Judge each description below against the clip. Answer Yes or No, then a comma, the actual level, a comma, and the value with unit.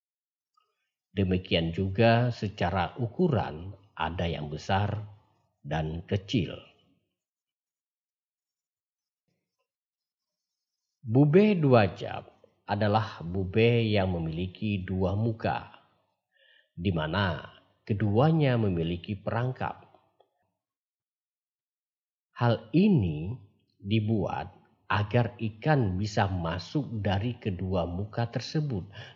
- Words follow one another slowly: Yes, slow, 70 wpm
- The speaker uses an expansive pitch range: No, average, 4.1 semitones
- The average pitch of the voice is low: Yes, low, 105 Hz